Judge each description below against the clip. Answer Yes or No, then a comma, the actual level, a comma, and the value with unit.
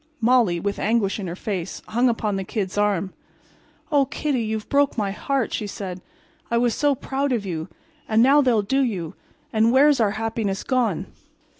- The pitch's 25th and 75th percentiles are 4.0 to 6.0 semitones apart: Yes, average, 4.5 semitones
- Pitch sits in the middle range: No, high, 220 Hz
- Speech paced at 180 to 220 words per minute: No, average, 170 wpm